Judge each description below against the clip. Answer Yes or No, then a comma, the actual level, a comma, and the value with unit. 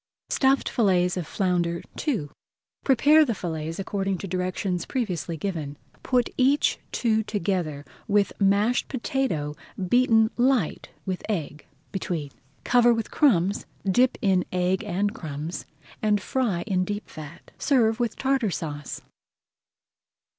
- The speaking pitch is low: No, high, 195 Hz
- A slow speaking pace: Yes, slow, 125 wpm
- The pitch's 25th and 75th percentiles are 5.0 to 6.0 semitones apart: Yes, wide, 5.5 semitones